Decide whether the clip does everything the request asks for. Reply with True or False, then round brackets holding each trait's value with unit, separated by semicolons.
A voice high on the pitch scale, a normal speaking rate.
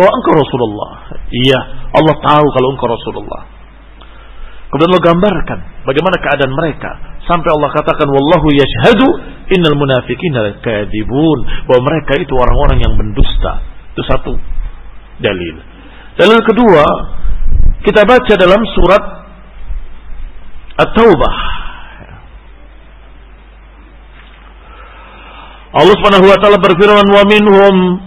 False (140 Hz; 100 wpm)